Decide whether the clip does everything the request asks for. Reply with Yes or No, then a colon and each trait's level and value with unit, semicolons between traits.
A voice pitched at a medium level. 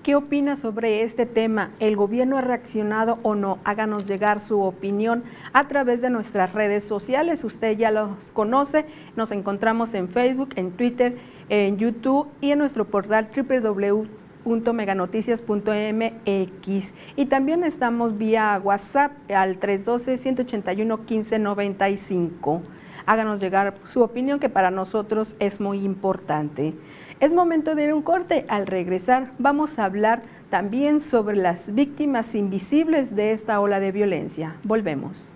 No: high, 220 Hz